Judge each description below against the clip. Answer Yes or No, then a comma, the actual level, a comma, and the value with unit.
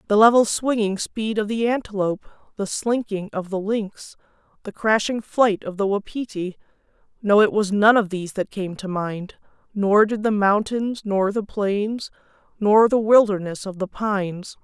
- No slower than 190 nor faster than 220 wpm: No, average, 165 wpm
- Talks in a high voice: Yes, high, 205 Hz